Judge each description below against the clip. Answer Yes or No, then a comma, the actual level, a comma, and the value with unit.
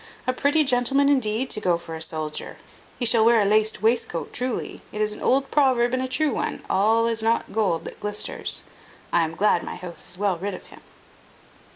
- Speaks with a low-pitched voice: No, high, 220 Hz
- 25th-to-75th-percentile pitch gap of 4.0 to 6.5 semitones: Yes, average, 4.4 semitones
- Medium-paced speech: No, fast, 210 wpm